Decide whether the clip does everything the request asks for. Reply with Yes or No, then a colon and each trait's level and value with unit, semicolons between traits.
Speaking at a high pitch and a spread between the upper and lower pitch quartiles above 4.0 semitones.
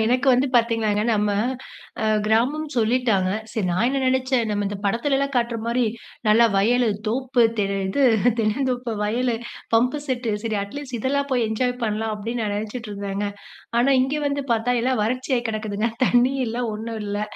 No: high, 235 Hz; average, 3.1 semitones